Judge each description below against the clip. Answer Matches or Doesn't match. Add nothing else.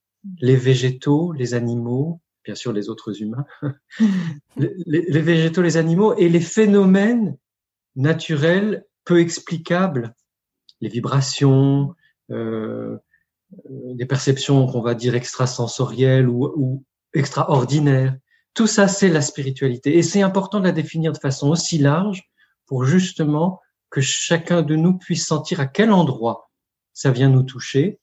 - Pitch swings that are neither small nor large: Matches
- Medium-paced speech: Doesn't match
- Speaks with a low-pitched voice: Doesn't match